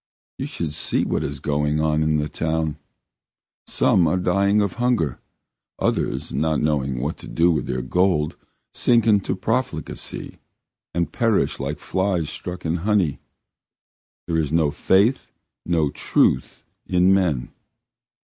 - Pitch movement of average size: Yes, average, 4.1 semitones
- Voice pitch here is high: No, very low, 80 Hz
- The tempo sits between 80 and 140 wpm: Yes, slow, 135 wpm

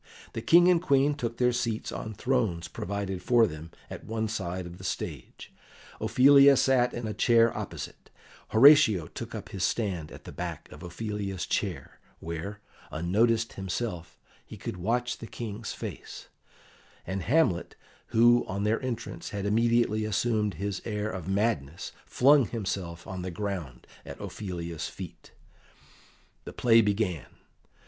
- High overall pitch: No, low, 105 Hz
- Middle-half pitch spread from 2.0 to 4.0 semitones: No, average, 4.4 semitones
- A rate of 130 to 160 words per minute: Yes, average, 145 wpm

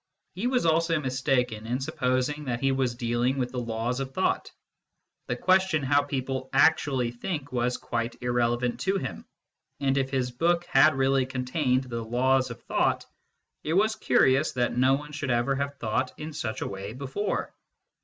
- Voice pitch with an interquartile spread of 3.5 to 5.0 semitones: No, average, 2.7 semitones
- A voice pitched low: Yes, low, 130 Hz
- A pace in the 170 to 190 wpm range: Yes, average, 175 wpm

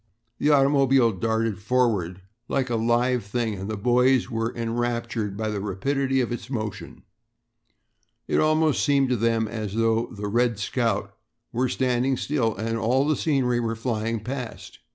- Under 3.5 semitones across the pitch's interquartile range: Yes, average, 2.8 semitones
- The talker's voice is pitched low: Yes, low, 115 Hz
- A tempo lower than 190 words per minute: Yes, average, 155 wpm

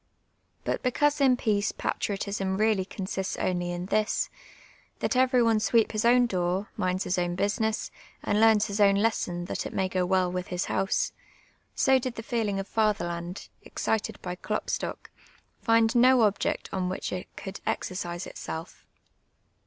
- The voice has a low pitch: No, high, 200 Hz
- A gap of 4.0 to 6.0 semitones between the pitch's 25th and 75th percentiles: No, average, 3.4 semitones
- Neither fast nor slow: Yes, average, 160 wpm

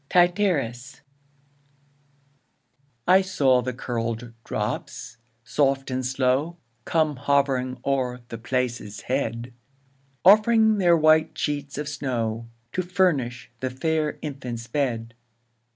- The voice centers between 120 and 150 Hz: Yes, low, 135 Hz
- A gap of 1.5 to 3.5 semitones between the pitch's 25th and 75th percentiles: No, average, 4.3 semitones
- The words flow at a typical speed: No, slow, 105 wpm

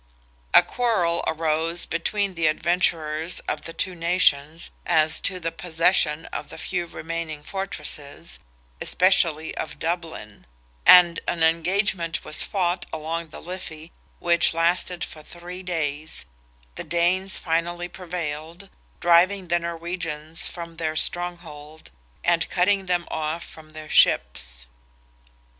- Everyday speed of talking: No, slow, 120 wpm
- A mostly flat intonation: Yes, narrow, 2.1 semitones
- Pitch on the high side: No, medium, 170 Hz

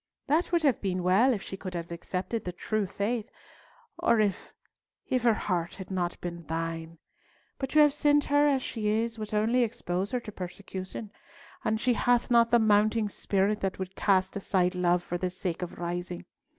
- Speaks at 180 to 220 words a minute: Yes, average, 190 wpm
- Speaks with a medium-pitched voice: No, high, 200 Hz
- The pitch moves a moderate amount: Yes, average, 4.5 semitones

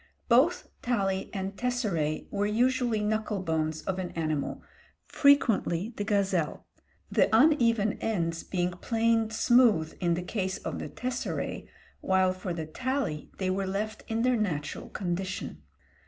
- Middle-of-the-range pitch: No, high, 200 Hz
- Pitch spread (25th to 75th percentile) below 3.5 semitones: No, average, 4.5 semitones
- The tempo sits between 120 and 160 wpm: Yes, average, 140 wpm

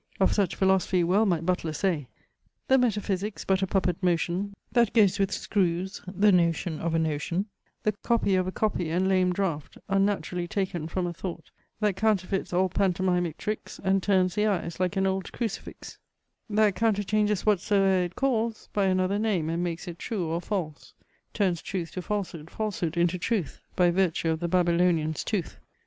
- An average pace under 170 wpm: No, average, 175 wpm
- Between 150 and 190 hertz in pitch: Yes, medium, 185 Hz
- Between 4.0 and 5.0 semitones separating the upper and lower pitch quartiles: No, average, 2.8 semitones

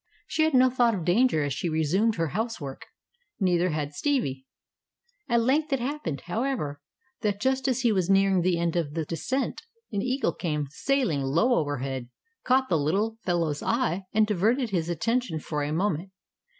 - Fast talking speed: No, average, 175 wpm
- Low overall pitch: No, high, 190 Hz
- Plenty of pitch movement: Yes, wide, 7.6 semitones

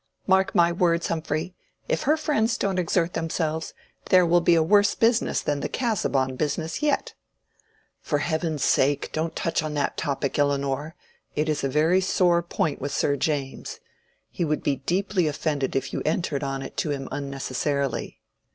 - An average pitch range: Yes, average, 3.8 semitones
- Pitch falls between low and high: Yes, medium, 160 Hz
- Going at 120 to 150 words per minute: No, average, 170 wpm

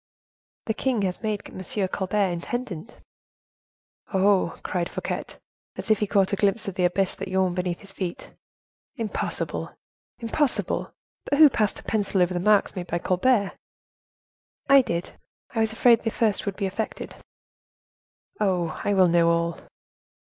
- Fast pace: No, average, 155 wpm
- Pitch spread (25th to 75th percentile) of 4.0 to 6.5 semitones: No, average, 3.3 semitones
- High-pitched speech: Yes, high, 195 Hz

